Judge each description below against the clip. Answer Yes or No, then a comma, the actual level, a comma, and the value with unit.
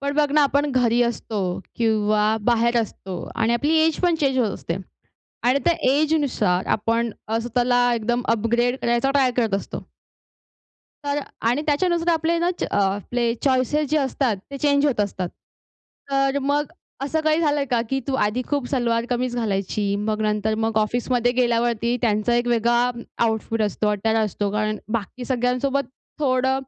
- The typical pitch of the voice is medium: No, high, 240 Hz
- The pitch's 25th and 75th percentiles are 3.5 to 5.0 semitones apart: Yes, average, 3.9 semitones